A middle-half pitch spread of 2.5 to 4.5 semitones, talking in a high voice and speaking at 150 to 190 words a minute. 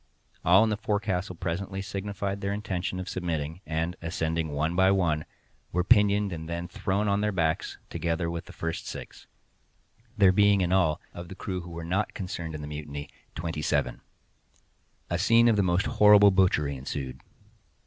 No: average, 3.4 semitones; very low, 90 Hz; average, 170 wpm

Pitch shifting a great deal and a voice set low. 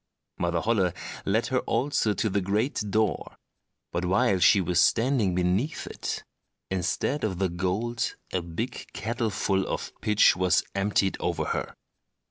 No: average, 3.8 semitones; low, 100 Hz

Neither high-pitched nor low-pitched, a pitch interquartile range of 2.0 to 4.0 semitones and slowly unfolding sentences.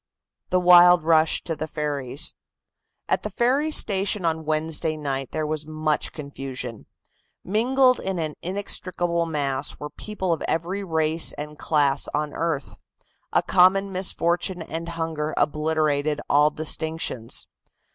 Yes: medium, 160 Hz; average, 3.0 semitones; slow, 130 wpm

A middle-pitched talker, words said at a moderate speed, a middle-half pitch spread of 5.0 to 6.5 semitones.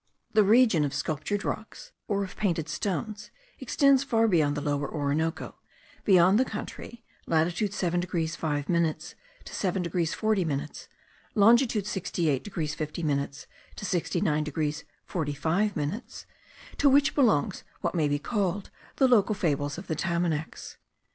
Yes: medium, 175 Hz; average, 145 wpm; average, 5.3 semitones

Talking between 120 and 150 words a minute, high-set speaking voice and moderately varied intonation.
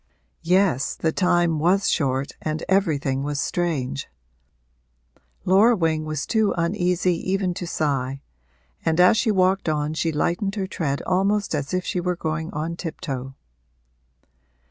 No: average, 140 wpm; medium, 170 Hz; average, 3.6 semitones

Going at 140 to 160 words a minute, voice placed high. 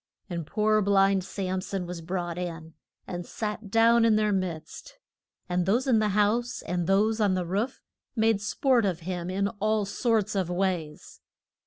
No: average, 170 wpm; high, 195 Hz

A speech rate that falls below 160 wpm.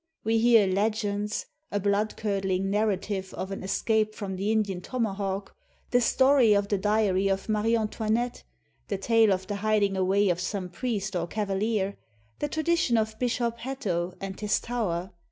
No: average, 165 wpm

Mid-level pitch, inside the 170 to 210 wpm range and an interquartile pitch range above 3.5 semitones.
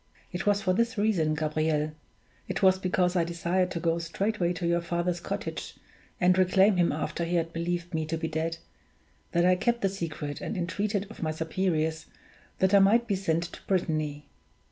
No: medium, 175 Hz; average, 190 wpm; average, 2.7 semitones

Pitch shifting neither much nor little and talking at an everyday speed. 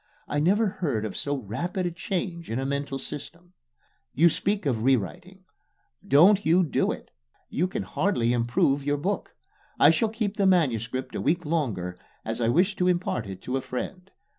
No: wide, 6.6 semitones; average, 180 wpm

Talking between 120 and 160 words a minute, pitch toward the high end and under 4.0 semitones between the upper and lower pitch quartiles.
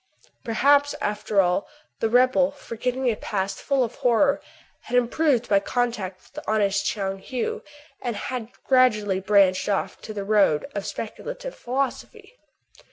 No: average, 145 wpm; high, 230 Hz; average, 4.3 semitones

